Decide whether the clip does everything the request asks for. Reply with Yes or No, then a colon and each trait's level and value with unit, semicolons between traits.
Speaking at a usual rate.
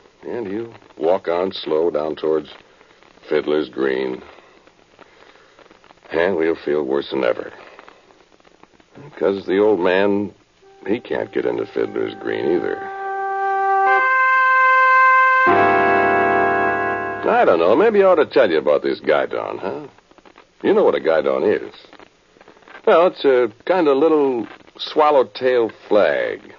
No: slow, 120 wpm